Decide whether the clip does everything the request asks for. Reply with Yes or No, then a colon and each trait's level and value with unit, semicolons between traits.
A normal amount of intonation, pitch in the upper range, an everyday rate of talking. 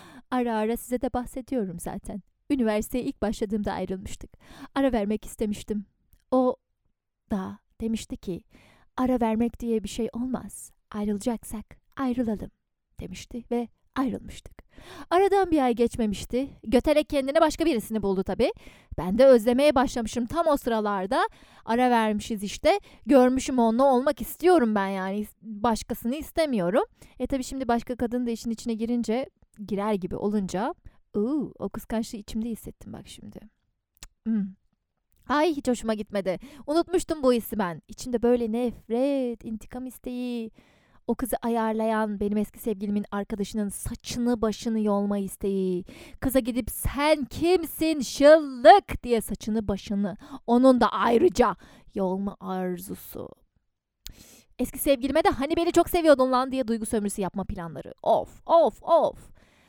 Yes: average, 3.9 semitones; high, 235 Hz; average, 130 wpm